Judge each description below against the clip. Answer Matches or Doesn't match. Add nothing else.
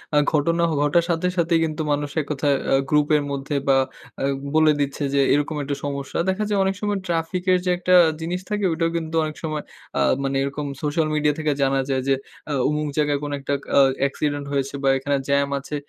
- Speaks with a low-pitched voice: Doesn't match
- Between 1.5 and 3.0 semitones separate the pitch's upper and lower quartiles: Matches